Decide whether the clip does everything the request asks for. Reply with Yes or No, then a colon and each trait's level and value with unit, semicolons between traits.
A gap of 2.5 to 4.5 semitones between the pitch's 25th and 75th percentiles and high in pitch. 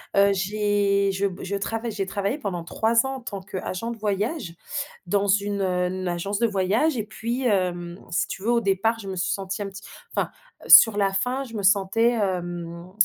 Yes: average, 2.8 semitones; high, 200 Hz